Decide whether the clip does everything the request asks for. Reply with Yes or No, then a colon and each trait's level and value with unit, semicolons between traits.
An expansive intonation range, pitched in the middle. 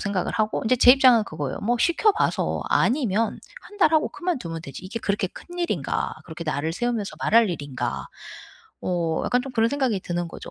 No: wide, 6.6 semitones; high, 220 Hz